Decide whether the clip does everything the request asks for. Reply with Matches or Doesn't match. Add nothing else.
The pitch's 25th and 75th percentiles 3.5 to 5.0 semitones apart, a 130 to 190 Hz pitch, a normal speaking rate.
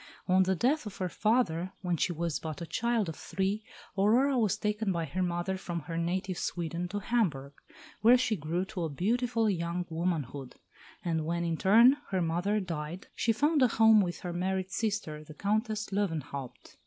Matches